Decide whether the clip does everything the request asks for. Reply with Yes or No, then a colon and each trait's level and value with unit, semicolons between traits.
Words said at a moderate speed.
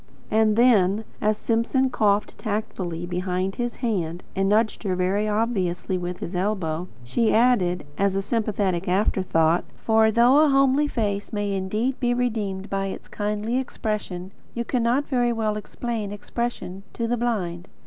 Yes: average, 155 wpm